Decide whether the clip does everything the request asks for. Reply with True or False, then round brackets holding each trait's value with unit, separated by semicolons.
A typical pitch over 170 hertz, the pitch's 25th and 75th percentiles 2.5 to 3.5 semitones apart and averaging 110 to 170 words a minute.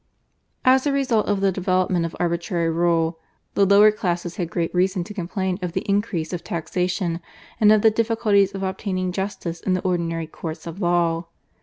False (185 Hz; 2.9 semitones; 180 wpm)